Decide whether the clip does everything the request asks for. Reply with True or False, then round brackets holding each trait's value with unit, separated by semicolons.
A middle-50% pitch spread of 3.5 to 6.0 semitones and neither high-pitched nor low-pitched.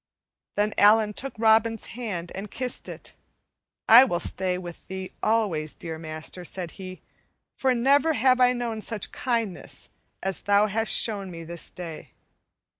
False (4.2 semitones; 210 Hz)